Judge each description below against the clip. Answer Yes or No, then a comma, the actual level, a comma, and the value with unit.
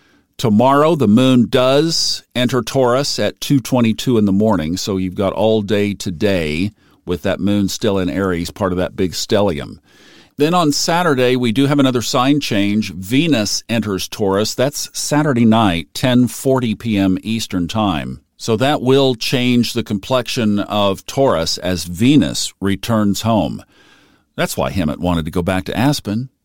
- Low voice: Yes, low, 110 Hz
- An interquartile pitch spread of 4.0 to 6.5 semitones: Yes, average, 4.7 semitones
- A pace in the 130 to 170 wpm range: Yes, average, 155 wpm